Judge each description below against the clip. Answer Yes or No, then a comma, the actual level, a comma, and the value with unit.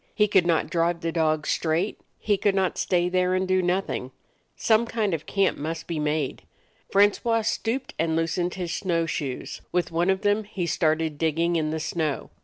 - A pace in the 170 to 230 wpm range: Yes, average, 200 wpm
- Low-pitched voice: No, medium, 175 Hz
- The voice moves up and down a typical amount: Yes, average, 3.2 semitones